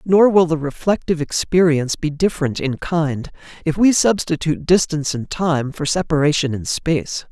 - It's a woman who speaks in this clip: No, male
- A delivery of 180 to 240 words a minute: No, average, 155 wpm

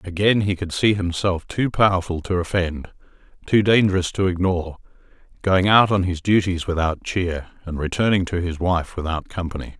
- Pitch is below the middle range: Yes, very low, 90 Hz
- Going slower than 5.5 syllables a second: Yes, 5.2 syllables/s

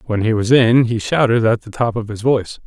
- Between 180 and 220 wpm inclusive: No, fast, 270 wpm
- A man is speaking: Yes, male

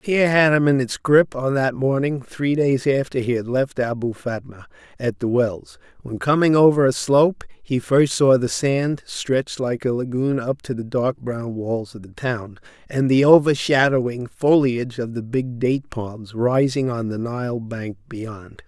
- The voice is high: No, low, 130 Hz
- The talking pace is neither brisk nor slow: Yes, average, 185 wpm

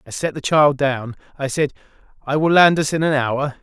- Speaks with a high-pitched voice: No, medium, 145 Hz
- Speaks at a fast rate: Yes, fast, 230 wpm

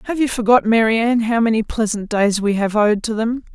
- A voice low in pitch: No, high, 225 Hz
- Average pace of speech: No, fast, 220 wpm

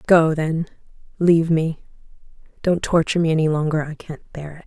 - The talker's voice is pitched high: No, medium, 160 Hz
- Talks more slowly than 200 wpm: Yes, average, 140 wpm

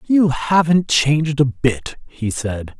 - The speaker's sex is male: Yes, male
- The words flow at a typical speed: Yes, average, 150 wpm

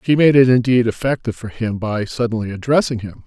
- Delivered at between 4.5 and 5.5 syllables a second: No, 6.0 syllables/s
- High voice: No, low, 120 Hz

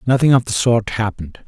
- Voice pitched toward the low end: Yes, low, 115 Hz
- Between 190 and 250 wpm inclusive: Yes, fast, 205 wpm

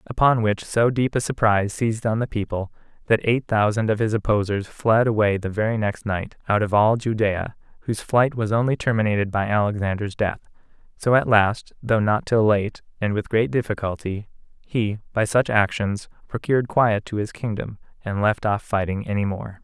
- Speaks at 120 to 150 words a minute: No, average, 185 wpm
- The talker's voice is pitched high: No, low, 110 Hz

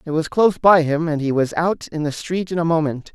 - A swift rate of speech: Yes, fast, 285 wpm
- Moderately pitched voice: Yes, medium, 160 Hz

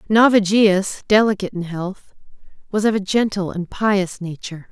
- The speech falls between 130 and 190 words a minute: Yes, average, 140 wpm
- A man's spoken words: No, female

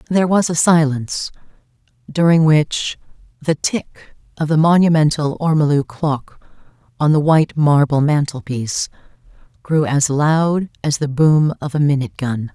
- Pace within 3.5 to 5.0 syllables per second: Yes, 4.6 syllables/s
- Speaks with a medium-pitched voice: Yes, medium, 150 Hz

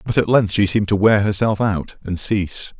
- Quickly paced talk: Yes, fast, 235 wpm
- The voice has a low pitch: Yes, low, 100 Hz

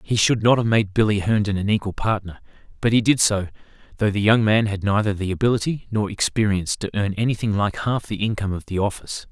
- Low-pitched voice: Yes, low, 105 Hz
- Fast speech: Yes, fast, 220 wpm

